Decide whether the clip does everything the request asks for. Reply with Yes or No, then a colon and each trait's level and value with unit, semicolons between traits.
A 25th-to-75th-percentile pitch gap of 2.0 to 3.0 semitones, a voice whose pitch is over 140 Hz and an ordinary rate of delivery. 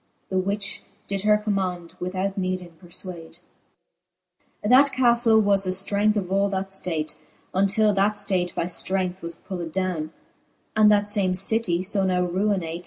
Yes: narrow, 2.4 semitones; high, 190 Hz; average, 155 wpm